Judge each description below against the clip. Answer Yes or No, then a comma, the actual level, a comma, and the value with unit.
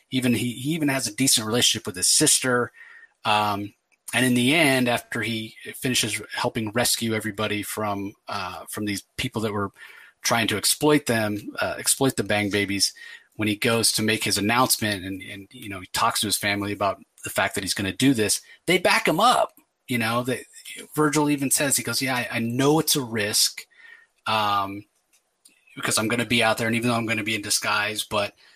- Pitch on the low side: Yes, low, 115 Hz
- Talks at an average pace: No, fast, 210 wpm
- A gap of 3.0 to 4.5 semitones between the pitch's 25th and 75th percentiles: Yes, average, 3.7 semitones